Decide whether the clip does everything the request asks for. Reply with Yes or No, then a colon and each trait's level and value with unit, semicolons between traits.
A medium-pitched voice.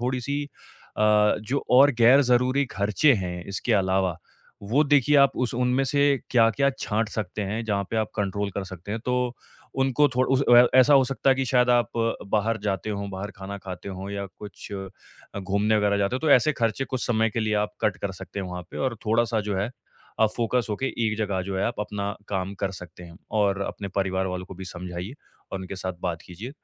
No: low, 105 Hz